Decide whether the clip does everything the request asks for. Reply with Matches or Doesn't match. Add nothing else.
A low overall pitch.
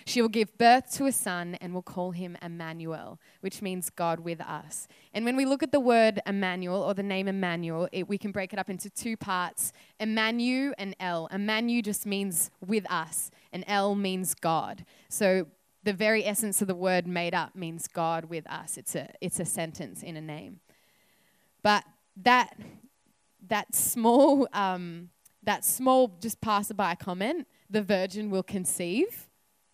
Doesn't match